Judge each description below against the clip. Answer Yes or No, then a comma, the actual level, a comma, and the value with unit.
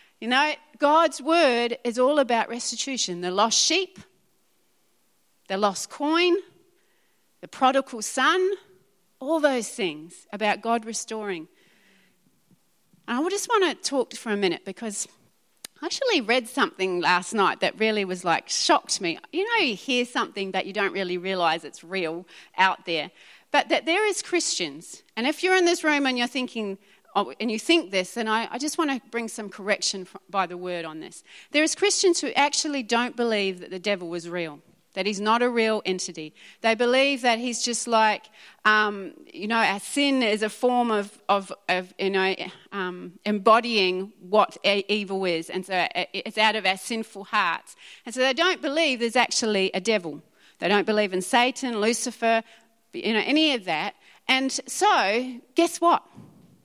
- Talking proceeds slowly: No, average, 175 wpm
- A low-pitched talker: No, high, 225 Hz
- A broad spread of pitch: Yes, wide, 6.3 semitones